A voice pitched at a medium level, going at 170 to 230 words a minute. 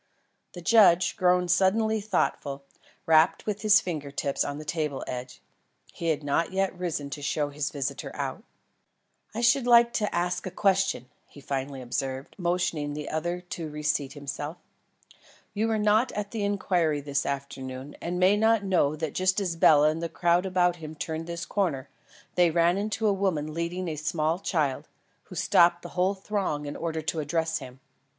Yes: medium, 170 Hz; average, 180 wpm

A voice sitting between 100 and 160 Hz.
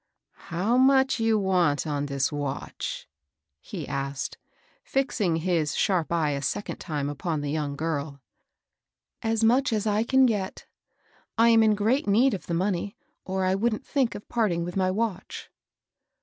No: medium, 185 Hz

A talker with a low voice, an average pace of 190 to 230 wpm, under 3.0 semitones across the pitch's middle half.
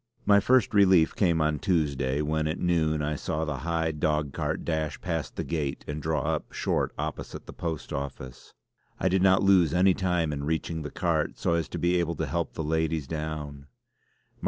Yes: very low, 80 Hz; average, 195 wpm; narrow, 2.4 semitones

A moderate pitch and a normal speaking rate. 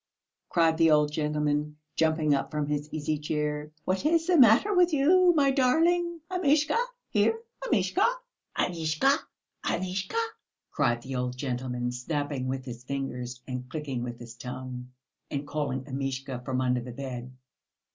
Yes: medium, 150 Hz; average, 145 wpm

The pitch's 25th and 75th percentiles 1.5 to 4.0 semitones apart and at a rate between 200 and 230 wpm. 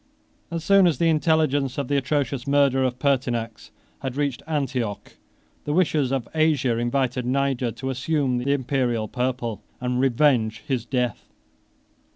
No: narrow, 2.6 semitones; average, 150 wpm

